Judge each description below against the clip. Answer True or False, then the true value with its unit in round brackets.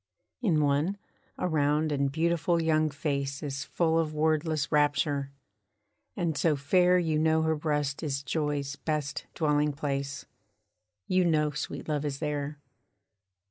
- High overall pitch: False (150 Hz)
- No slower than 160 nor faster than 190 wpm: False (140 wpm)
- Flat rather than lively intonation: True (1.9 semitones)